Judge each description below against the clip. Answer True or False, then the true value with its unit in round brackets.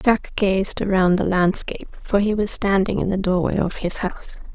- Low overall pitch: False (190 Hz)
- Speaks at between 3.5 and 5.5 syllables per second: True (5.0 syllables/s)